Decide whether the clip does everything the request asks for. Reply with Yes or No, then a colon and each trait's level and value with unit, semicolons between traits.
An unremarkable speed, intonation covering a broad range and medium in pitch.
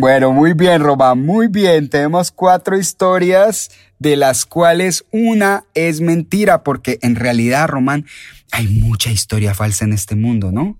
Yes: average, 150 wpm; wide, 7.3 semitones; medium, 145 Hz